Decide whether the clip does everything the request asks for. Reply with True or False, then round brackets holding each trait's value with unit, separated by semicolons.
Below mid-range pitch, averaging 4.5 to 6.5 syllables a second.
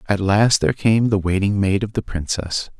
True (100 Hz; 5.1 syllables/s)